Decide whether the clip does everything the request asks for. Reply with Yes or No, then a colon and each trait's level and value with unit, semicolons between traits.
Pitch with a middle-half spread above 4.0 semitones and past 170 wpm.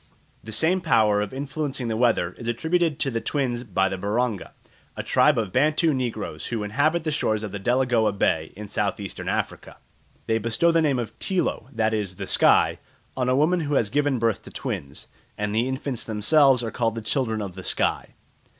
Yes: average, 5.0 semitones; average, 195 wpm